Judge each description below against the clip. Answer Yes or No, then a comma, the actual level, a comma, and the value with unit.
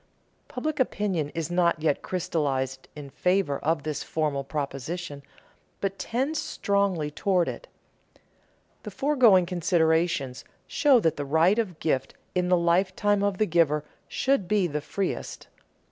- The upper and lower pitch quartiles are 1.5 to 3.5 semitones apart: No, average, 4.8 semitones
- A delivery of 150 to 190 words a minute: No, average, 140 wpm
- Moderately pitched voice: Yes, medium, 175 Hz